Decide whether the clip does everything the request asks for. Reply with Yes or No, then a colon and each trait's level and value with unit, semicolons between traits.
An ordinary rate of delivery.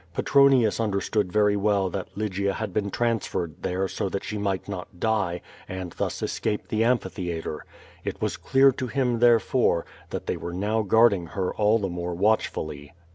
Yes: average, 175 wpm